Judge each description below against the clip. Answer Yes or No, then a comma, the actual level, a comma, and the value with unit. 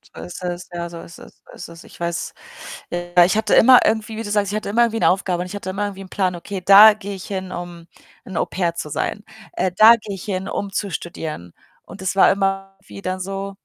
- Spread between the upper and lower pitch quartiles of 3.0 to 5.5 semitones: No, narrow, 2.5 semitones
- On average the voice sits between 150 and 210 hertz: Yes, high, 190 Hz